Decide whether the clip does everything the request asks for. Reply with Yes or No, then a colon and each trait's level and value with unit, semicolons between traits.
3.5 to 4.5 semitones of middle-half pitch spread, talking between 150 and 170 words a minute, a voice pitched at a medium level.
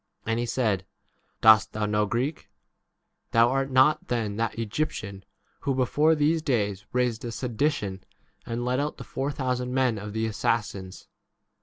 No: average, 3.9 semitones; average, 165 wpm; low, 120 Hz